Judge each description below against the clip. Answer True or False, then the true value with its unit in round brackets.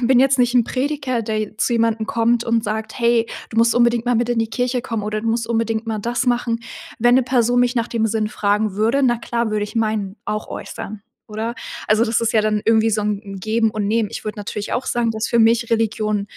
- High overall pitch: True (225 Hz)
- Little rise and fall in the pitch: True (1.8 semitones)